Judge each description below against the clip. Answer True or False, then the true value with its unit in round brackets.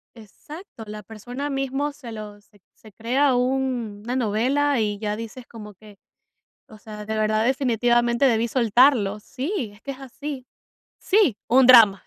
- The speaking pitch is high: True (235 Hz)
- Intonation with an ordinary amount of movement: True (3.8 semitones)